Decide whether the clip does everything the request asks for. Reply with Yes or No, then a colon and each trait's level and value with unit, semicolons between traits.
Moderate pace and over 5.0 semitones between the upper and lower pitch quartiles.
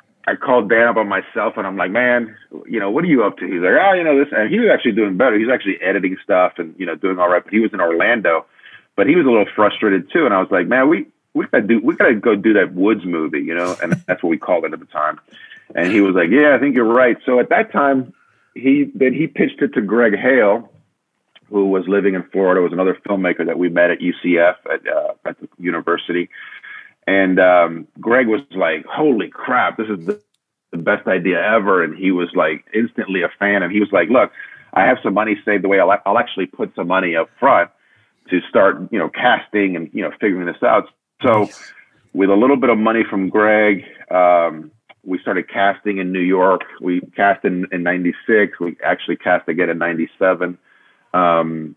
No: fast, 230 wpm; wide, 5.4 semitones